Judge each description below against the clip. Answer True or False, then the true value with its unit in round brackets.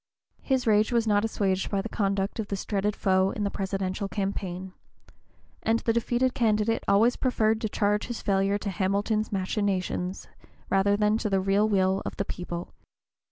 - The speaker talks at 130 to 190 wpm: True (170 wpm)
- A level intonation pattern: True (2.0 semitones)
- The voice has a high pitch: True (205 Hz)